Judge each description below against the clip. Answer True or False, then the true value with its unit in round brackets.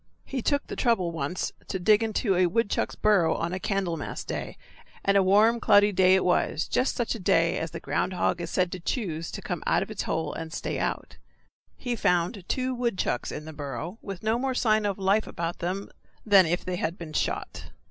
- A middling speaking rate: False (215 wpm)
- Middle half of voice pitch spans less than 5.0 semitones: True (4.2 semitones)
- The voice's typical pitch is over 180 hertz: True (190 Hz)